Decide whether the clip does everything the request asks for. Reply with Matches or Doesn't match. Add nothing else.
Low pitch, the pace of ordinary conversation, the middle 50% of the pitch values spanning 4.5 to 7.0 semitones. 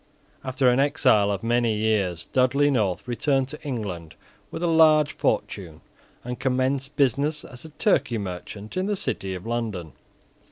Matches